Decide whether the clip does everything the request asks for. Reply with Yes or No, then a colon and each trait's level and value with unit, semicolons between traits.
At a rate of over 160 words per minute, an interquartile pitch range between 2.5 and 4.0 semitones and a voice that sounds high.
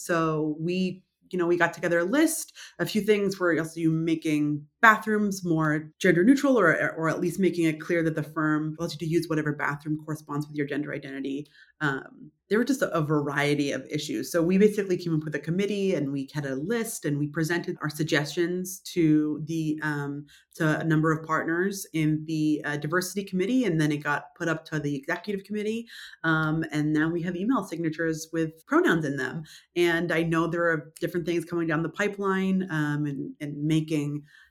No: fast, 205 wpm; average, 2.8 semitones; medium, 160 Hz